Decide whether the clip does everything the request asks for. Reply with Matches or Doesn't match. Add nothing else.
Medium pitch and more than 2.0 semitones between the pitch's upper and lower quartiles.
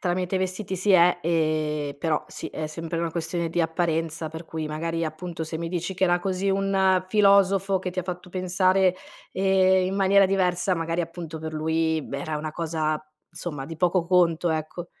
Matches